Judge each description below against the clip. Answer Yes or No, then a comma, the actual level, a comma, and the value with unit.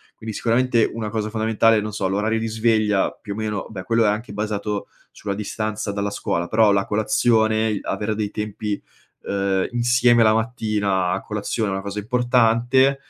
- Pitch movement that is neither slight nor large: No, narrow, 1.8 semitones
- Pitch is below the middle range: Yes, low, 110 Hz